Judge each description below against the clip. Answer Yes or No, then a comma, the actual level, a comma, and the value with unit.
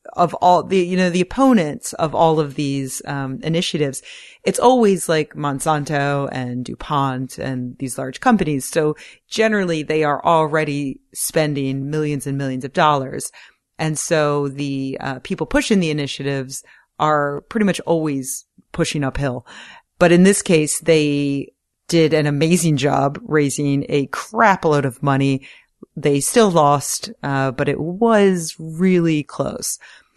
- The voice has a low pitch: No, medium, 150 Hz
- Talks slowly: No, average, 145 wpm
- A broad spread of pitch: No, average, 3.5 semitones